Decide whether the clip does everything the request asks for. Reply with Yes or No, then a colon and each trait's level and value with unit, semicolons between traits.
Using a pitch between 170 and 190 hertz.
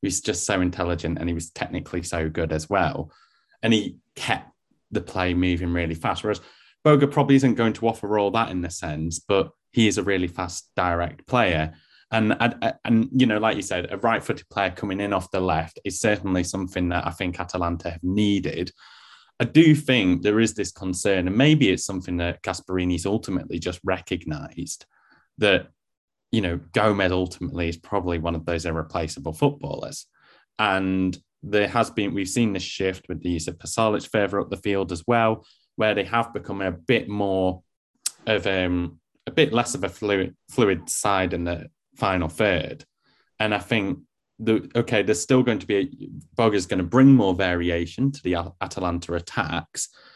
No: very low, 95 Hz